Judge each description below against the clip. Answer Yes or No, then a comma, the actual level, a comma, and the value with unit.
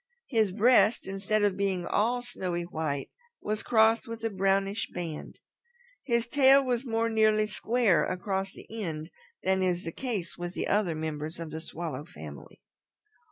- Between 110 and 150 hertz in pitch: No, high, 195 Hz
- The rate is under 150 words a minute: No, average, 155 wpm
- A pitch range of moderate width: Yes, average, 4.7 semitones